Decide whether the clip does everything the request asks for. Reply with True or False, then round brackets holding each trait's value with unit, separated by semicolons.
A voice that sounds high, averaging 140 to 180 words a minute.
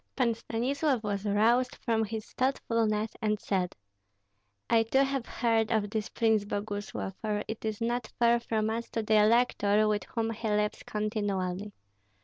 True (220 Hz; 155 wpm)